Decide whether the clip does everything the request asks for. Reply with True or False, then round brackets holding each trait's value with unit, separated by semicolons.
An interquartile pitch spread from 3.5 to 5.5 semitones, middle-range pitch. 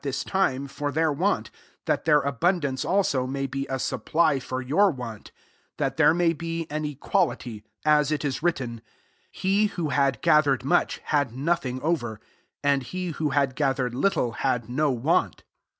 True (4.2 semitones; 145 Hz)